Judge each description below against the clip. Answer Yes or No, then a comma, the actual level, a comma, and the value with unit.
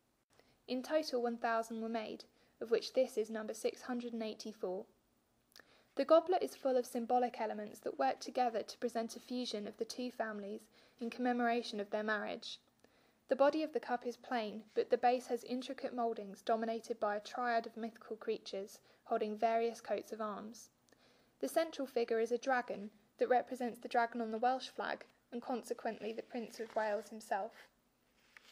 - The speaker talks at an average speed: Yes, average, 170 wpm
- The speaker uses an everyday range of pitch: No, narrow, 2.1 semitones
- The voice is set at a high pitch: Yes, high, 235 Hz